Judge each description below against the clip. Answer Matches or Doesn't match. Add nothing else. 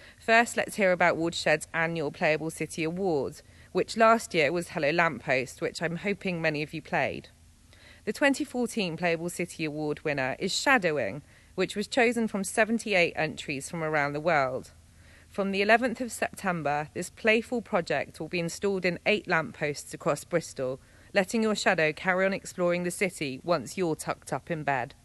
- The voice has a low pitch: Doesn't match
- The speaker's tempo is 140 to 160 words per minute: Doesn't match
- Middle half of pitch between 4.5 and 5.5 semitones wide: Matches